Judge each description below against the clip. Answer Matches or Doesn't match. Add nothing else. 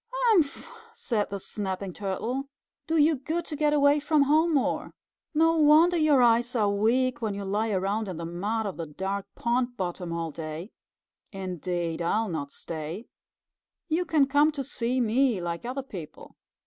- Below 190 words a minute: Matches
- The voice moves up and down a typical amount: Doesn't match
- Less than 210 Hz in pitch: Doesn't match